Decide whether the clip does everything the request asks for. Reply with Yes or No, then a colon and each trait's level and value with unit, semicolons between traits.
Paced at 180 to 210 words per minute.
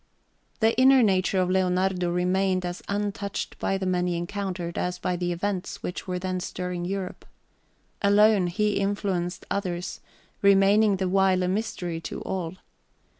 No: average, 150 wpm